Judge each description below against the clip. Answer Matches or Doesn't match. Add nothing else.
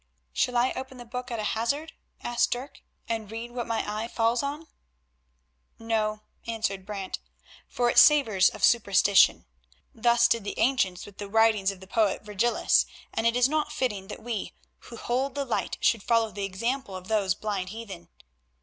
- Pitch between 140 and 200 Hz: Doesn't match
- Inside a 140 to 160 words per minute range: Doesn't match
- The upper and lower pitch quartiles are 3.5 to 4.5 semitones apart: Doesn't match